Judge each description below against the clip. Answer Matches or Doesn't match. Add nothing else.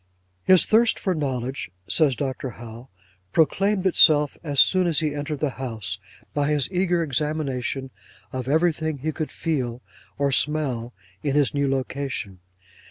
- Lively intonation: Doesn't match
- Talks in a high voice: Doesn't match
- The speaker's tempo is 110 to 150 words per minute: Matches